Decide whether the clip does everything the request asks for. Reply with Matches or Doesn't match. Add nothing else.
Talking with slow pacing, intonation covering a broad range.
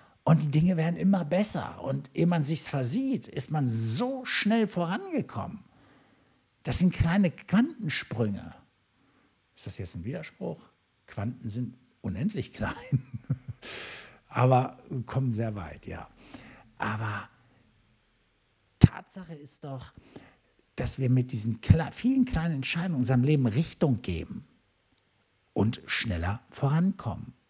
Matches